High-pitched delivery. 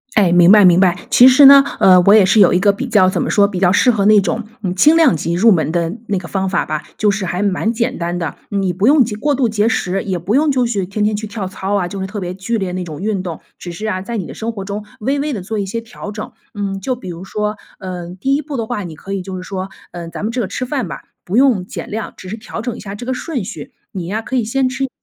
Yes: high, 205 Hz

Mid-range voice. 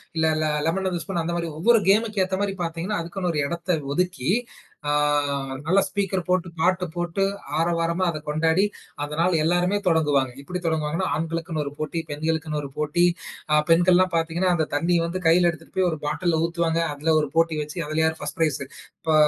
Yes: medium, 165 Hz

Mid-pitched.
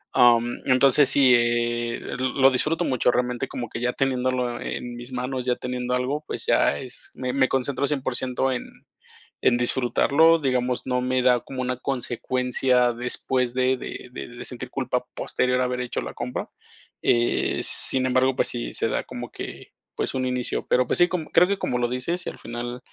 No: low, 125 Hz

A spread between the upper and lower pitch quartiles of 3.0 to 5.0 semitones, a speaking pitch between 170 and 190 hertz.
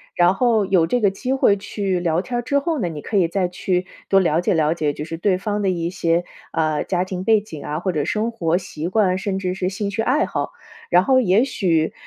Yes: average, 3.6 semitones; medium, 185 Hz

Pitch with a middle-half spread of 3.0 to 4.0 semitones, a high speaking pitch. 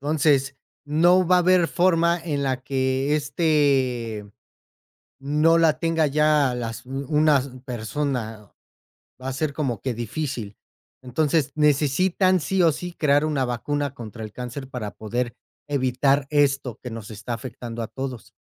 No: average, 3.6 semitones; medium, 140 Hz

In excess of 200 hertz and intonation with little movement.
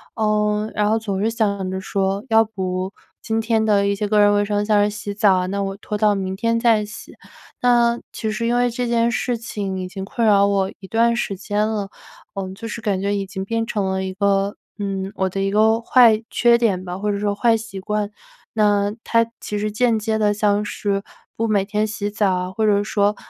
Yes: high, 210 Hz; narrow, 2.0 semitones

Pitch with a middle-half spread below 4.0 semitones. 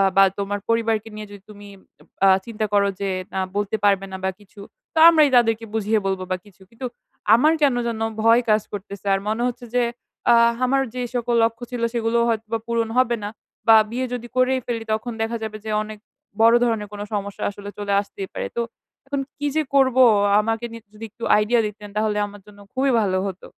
Yes: narrow, 2.6 semitones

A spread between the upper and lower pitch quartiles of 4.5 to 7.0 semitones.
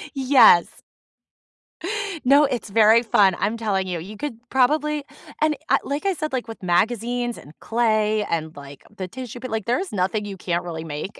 Yes: average, 5.3 semitones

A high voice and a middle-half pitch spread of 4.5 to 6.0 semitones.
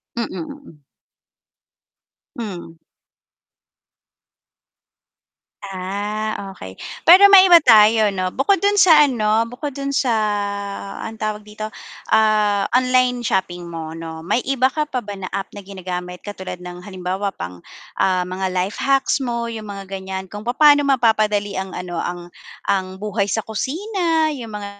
Yes: high, 210 Hz; average, 5.2 semitones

